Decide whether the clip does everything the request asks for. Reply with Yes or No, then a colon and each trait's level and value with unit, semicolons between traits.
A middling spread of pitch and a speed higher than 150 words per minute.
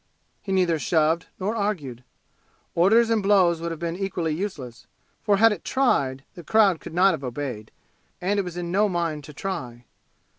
Yes: average, 4.6 semitones; average, 180 wpm